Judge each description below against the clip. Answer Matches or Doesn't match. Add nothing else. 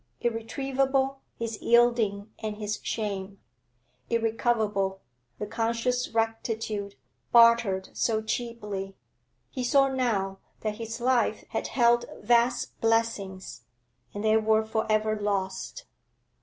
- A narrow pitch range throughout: Matches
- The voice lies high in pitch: Matches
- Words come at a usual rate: Doesn't match